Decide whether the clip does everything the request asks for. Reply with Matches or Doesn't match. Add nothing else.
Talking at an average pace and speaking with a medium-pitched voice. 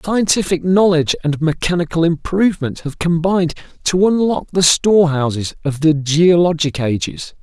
Doesn't match